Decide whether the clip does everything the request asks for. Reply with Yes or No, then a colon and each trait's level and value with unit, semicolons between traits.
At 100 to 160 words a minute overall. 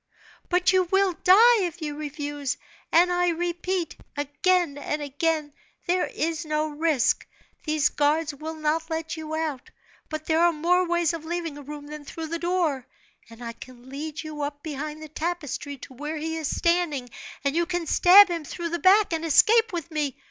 No: average, 185 wpm